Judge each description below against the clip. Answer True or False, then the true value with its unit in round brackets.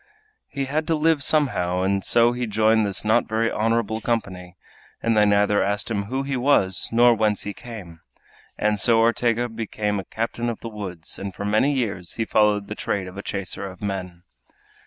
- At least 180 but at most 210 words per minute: True (190 wpm)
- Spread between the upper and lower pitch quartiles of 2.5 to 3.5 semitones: True (2.9 semitones)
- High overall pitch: False (110 Hz)